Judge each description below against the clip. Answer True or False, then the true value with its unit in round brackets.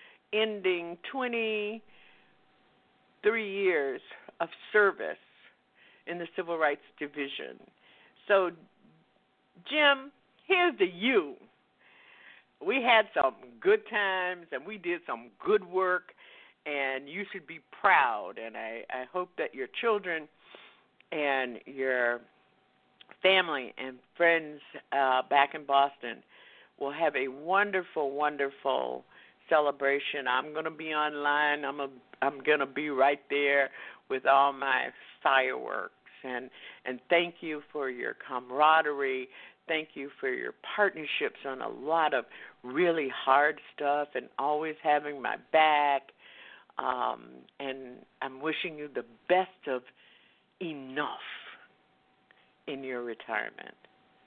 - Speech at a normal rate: False (115 wpm)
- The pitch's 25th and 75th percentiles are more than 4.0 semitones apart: True (5.4 semitones)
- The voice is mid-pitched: True (150 Hz)